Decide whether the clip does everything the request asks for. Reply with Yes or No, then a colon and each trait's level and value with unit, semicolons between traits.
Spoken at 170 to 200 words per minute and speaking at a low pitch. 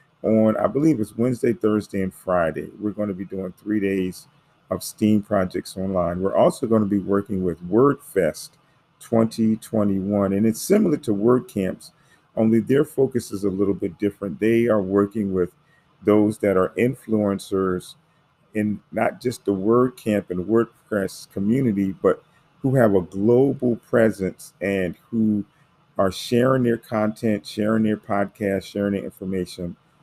No: average, 150 wpm; low, 105 Hz